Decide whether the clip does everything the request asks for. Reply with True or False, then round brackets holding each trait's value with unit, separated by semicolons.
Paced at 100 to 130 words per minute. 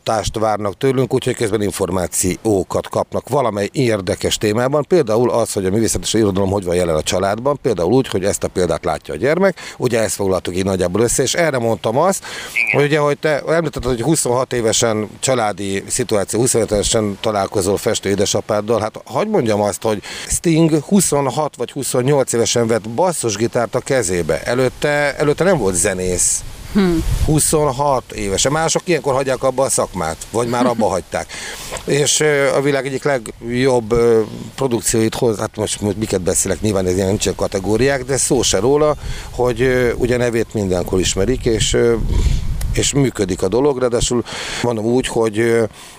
False (155 wpm)